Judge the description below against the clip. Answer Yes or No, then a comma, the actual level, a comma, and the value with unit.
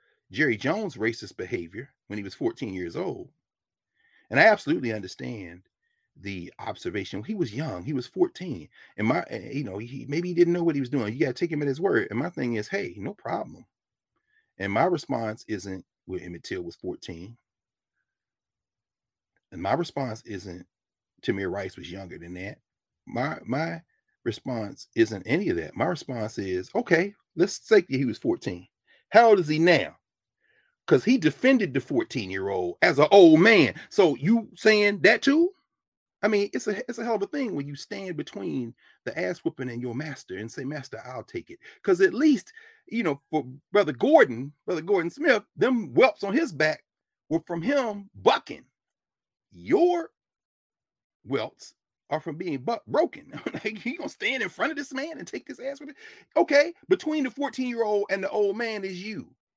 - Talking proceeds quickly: No, average, 185 wpm